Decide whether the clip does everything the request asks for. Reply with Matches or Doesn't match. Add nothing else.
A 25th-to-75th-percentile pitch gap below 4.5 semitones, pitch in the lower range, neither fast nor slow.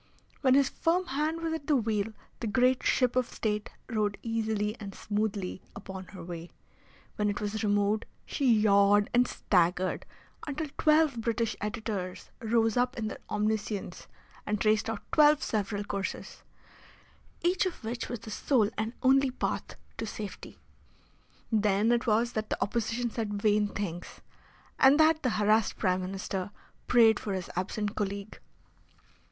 Doesn't match